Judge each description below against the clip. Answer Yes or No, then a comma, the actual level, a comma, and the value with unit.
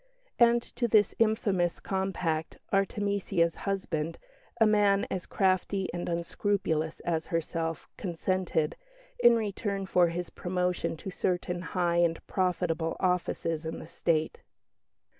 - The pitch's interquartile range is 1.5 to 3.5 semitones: Yes, average, 2.9 semitones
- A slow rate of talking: Yes, slow, 120 wpm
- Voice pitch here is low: No, medium, 180 Hz